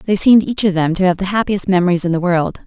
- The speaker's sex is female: Yes, female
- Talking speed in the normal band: No, fast, 295 wpm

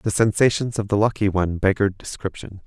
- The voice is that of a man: Yes, male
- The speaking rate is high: No, average, 180 wpm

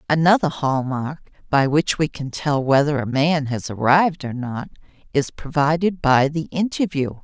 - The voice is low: No, medium, 145 Hz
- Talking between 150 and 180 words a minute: Yes, average, 165 wpm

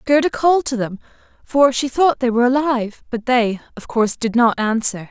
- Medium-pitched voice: No, high, 245 Hz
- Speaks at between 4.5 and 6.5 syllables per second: Yes, 5.5 syllables/s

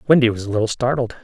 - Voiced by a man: Yes, male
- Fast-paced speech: Yes, fast, 245 wpm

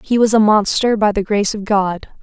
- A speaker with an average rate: No, fast, 245 wpm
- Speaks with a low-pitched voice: No, high, 210 Hz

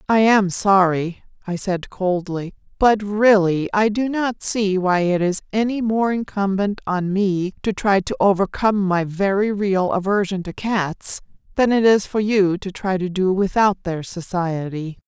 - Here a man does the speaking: No, female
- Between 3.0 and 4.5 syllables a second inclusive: Yes, 4.2 syllables/s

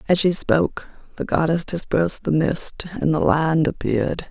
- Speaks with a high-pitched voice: No, medium, 160 Hz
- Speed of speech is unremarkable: Yes, average, 165 wpm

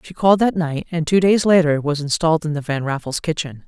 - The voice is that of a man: No, female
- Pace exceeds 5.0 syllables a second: Yes, 6.0 syllables/s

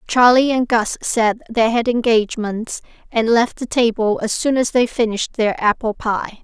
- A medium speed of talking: Yes, average, 175 wpm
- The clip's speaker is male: No, female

